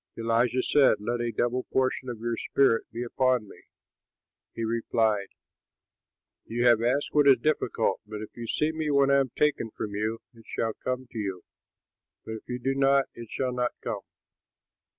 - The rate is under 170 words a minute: No, average, 180 wpm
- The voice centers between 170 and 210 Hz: No, low, 120 Hz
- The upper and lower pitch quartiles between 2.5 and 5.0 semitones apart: Yes, average, 2.8 semitones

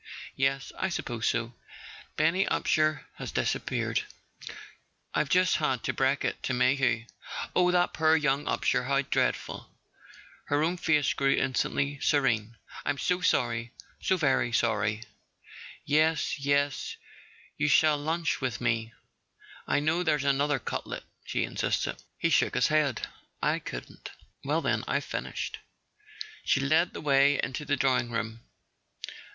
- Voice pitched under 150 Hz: Yes, medium, 140 Hz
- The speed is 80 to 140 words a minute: Yes, slow, 135 wpm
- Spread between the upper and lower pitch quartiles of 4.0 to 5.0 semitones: No, average, 3.4 semitones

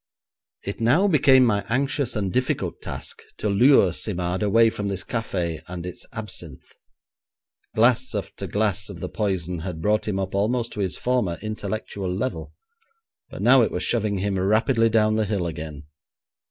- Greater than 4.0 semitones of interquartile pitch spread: No, average, 3.7 semitones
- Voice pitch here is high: No, low, 105 Hz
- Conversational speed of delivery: Yes, average, 165 wpm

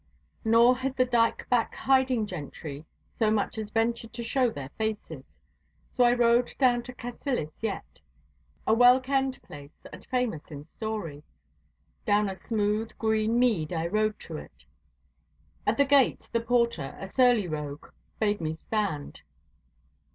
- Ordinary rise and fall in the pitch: Yes, average, 4.3 semitones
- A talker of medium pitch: No, high, 220 Hz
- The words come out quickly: No, average, 150 wpm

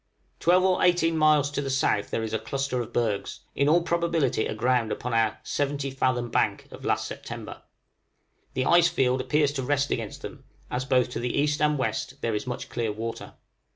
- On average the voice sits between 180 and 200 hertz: No, low, 135 Hz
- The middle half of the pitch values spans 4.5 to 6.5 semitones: No, average, 3.8 semitones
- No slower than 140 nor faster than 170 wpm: No, average, 195 wpm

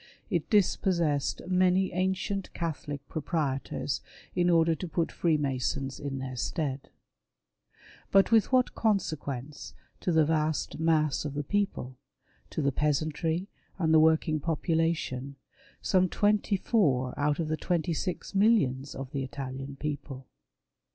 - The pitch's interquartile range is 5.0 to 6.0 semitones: No, average, 4.4 semitones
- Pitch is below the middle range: No, medium, 155 Hz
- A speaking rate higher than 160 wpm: No, slow, 135 wpm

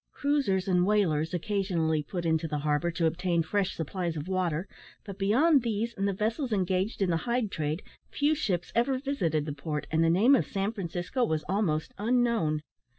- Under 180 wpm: No, average, 185 wpm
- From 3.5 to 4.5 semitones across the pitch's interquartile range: No, average, 5.2 semitones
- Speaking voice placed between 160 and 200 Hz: Yes, medium, 185 Hz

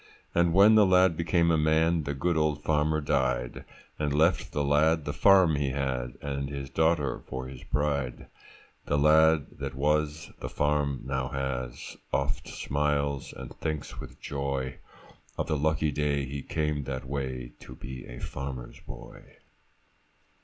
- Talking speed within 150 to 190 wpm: Yes, average, 155 wpm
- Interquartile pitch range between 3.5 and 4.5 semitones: No, narrow, 2.6 semitones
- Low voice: Yes, very low, 70 Hz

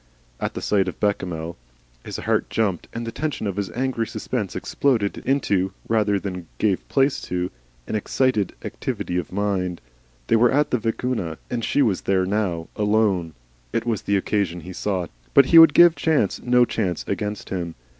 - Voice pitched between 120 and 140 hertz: No, low, 105 Hz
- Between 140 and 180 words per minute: Yes, average, 175 wpm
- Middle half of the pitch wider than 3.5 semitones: Yes, average, 4.4 semitones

